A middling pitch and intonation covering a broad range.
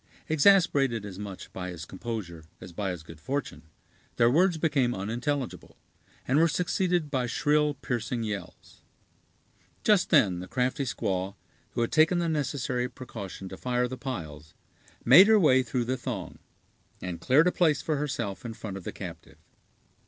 No: low, 125 Hz; wide, 7.0 semitones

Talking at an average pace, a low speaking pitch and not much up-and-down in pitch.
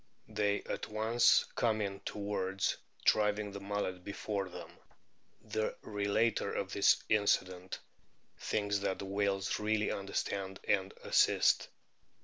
No: slow, 120 wpm; low, 100 Hz; narrow, 1.5 semitones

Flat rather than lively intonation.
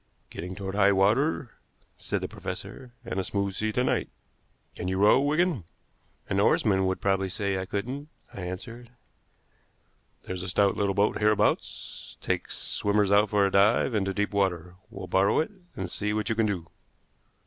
Yes: narrow, 2.1 semitones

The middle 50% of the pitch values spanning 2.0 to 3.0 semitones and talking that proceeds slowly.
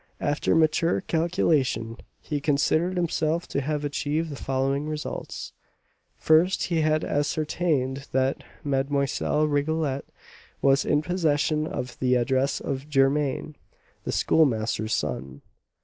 Yes: narrow, 2.6 semitones; slow, 115 wpm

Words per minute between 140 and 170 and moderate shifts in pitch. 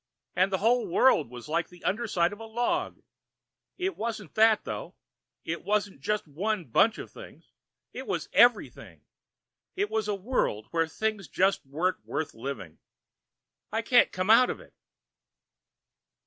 Yes: average, 150 wpm; average, 5.0 semitones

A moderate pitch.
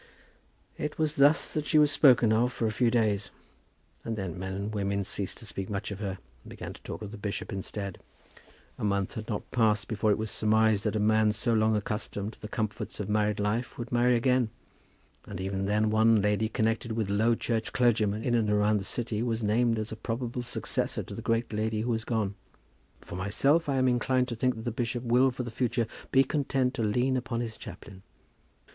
No: low, 110 Hz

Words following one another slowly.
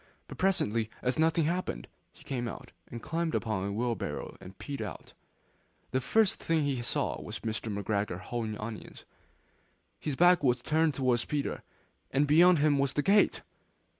No: average, 165 wpm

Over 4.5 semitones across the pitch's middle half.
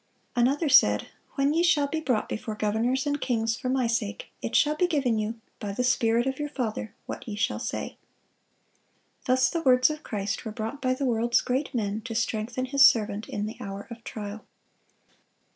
No: average, 4.0 semitones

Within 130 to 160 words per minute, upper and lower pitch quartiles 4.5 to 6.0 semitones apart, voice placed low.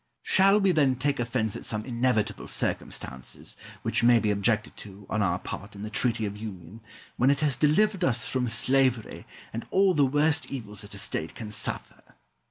No: average, 185 wpm; average, 5.0 semitones; low, 120 Hz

